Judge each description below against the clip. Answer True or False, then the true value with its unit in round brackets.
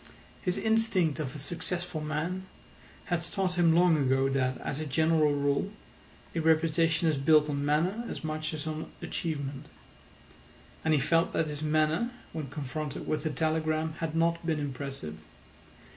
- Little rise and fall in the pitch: True (2.2 semitones)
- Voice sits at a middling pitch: True (155 Hz)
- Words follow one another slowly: False (160 wpm)